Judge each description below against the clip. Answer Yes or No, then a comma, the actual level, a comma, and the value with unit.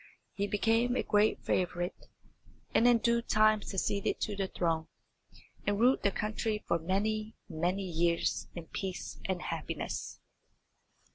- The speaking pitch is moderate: No, high, 200 Hz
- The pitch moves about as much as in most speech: Yes, average, 3.3 semitones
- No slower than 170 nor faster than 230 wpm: No, slow, 135 wpm